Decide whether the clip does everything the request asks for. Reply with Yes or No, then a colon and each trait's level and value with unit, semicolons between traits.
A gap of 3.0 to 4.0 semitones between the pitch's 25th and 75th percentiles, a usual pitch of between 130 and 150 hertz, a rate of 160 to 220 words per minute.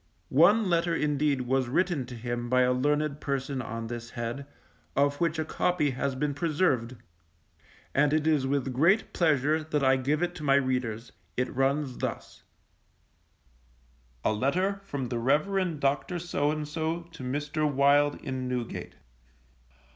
No: average, 3.4 semitones; medium, 140 Hz; average, 145 wpm